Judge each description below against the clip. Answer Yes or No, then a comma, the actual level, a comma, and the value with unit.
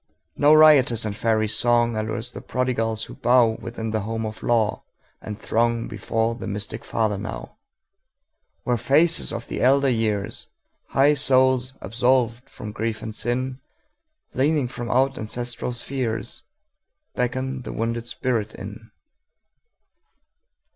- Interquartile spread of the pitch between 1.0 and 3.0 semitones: Yes, average, 2.7 semitones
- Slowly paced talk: Yes, slow, 110 wpm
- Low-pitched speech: Yes, low, 120 Hz